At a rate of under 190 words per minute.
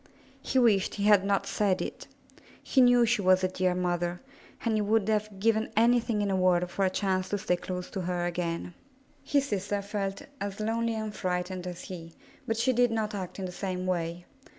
No: fast, 205 wpm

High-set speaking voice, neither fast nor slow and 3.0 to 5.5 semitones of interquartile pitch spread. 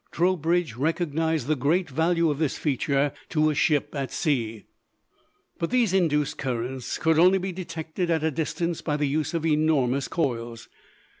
No: medium, 155 Hz; average, 160 wpm; average, 3.3 semitones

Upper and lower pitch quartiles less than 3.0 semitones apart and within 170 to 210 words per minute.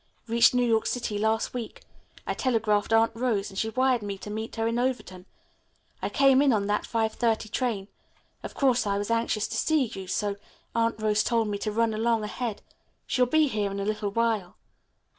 Yes: narrow, 2.4 semitones; average, 200 wpm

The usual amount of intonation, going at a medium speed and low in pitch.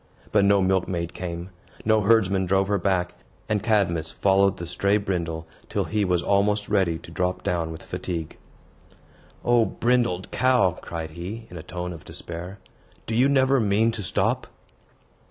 Yes: average, 3.5 semitones; average, 160 wpm; very low, 95 Hz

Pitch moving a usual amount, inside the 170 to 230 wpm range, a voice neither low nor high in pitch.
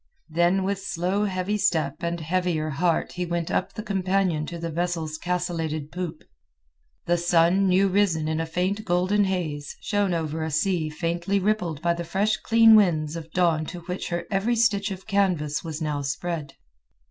Yes: average, 3.2 semitones; average, 175 wpm; medium, 175 Hz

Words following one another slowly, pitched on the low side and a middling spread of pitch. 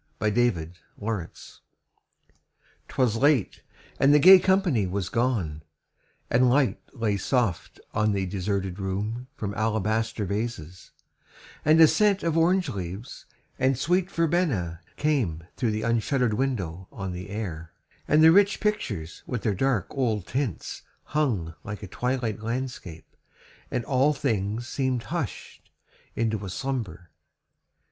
No: slow, 130 wpm; low, 115 Hz; wide, 5.8 semitones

